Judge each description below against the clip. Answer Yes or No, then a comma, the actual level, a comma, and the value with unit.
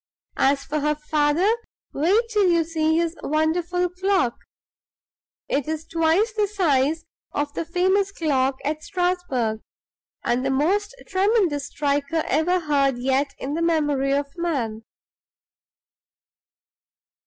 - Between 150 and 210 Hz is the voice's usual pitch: No, very high, 315 Hz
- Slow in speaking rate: Yes, slow, 120 wpm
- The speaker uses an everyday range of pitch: Yes, average, 4.1 semitones